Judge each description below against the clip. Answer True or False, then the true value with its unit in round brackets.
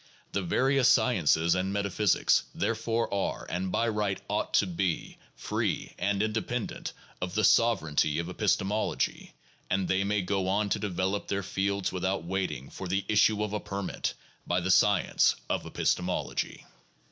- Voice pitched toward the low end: True (100 Hz)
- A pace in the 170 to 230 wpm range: False (150 wpm)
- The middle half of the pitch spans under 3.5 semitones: True (2.4 semitones)